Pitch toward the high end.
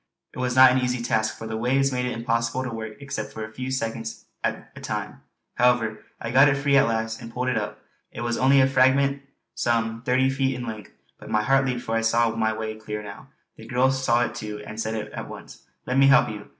No: low, 120 Hz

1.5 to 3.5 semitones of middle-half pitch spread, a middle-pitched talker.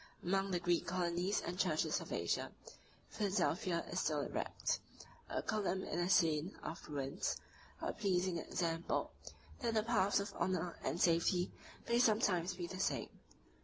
Yes: narrow, 2.6 semitones; medium, 180 Hz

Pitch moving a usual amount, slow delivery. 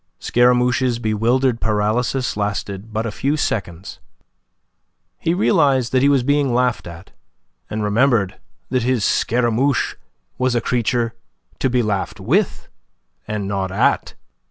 Yes: average, 3.4 semitones; slow, 130 wpm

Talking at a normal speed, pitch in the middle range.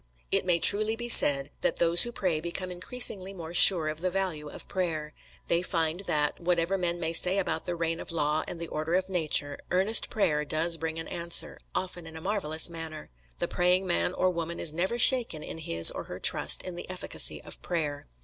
No: fast, 210 wpm; medium, 170 Hz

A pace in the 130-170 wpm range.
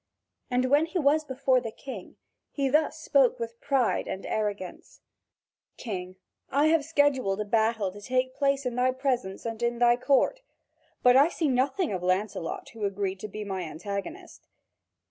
Yes: average, 165 wpm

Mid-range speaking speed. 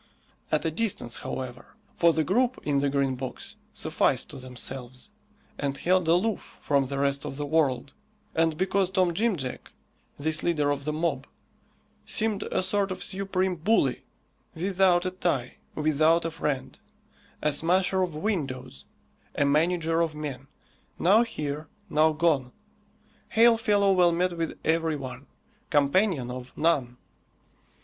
Yes: average, 145 wpm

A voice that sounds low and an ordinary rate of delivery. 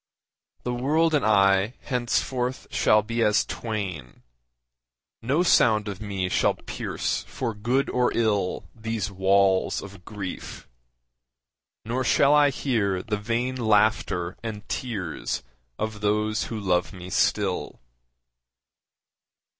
No: low, 105 Hz; slow, 115 wpm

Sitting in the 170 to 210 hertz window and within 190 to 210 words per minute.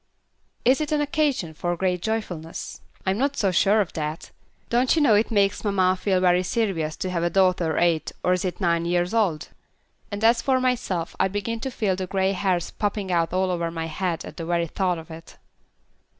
Yes: medium, 185 Hz; fast, 205 wpm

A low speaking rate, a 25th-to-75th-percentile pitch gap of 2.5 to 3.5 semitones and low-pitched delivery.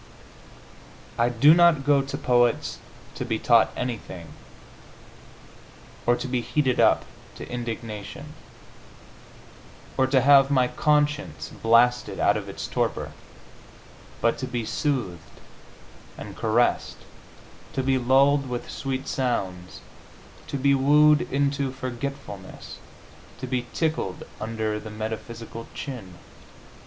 Yes: slow, 115 wpm; average, 3.2 semitones; low, 125 Hz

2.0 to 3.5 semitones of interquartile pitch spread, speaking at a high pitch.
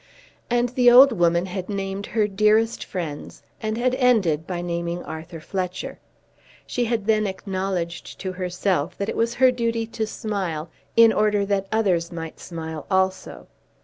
No: average, 4.3 semitones; high, 195 Hz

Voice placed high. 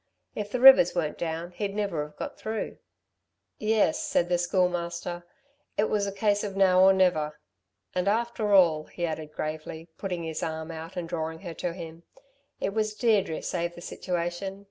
No: medium, 180 Hz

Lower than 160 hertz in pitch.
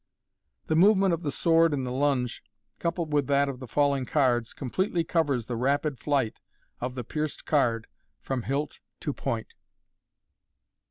Yes: medium, 140 Hz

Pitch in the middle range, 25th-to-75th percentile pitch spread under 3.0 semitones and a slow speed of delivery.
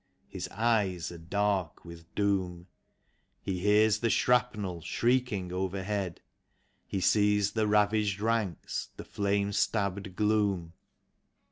No: low, 100 Hz; narrow, 2.5 semitones; slow, 110 wpm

